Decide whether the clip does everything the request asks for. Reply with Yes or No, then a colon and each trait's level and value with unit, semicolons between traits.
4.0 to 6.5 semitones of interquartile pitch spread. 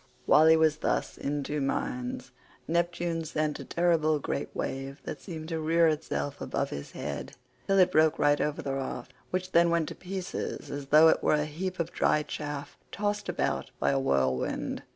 No: average, 2.8 semitones